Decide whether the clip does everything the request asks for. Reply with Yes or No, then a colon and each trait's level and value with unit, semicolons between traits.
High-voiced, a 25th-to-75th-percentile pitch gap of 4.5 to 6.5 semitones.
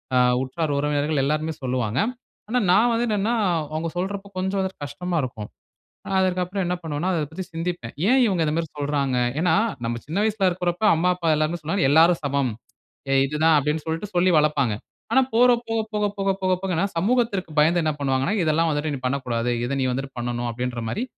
No: medium, 160 Hz; average, 4.9 semitones